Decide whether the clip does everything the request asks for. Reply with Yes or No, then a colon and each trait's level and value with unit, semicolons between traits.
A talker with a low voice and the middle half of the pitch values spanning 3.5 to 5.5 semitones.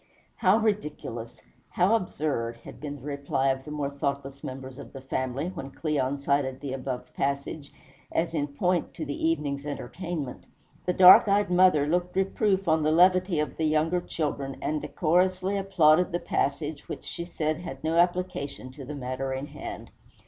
No: medium, 150 Hz; average, 4.3 semitones